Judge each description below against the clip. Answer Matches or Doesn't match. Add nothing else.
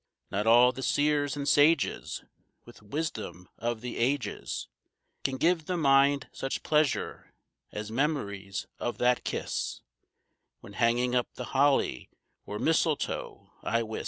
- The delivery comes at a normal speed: Doesn't match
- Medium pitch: Doesn't match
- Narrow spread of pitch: Doesn't match